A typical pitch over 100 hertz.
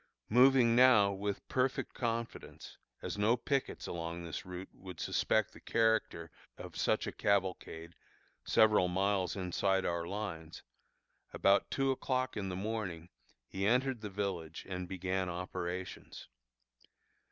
No: very low, 95 Hz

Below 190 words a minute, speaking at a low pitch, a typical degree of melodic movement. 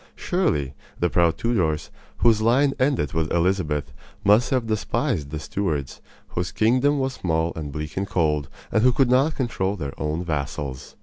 No: average, 165 wpm; very low, 90 Hz; wide, 7.7 semitones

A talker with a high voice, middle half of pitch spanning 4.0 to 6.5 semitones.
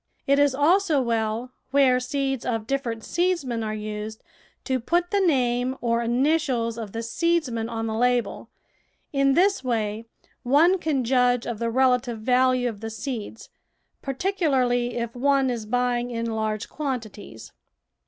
No: high, 245 Hz; average, 3.2 semitones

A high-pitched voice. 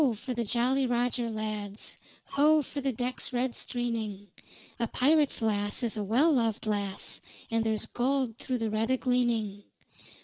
Yes: high, 235 Hz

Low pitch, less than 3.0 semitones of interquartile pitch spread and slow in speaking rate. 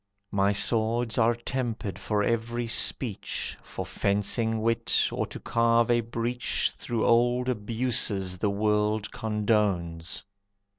Yes: low, 110 Hz; narrow, 2.4 semitones; slow, 115 wpm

